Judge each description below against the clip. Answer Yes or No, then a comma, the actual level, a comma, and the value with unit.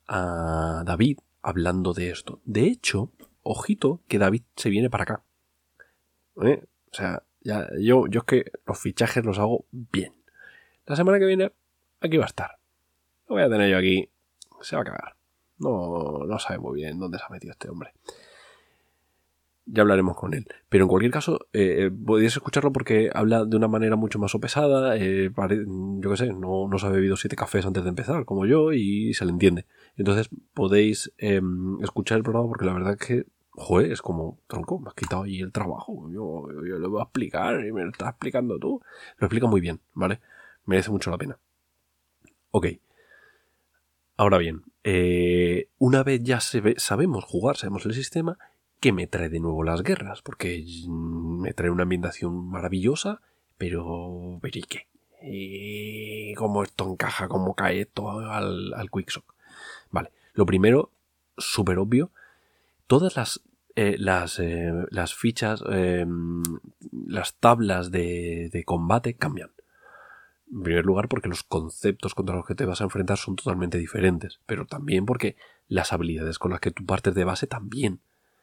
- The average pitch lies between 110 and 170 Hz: No, very low, 95 Hz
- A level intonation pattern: No, average, 3.9 semitones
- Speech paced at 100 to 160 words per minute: No, average, 170 wpm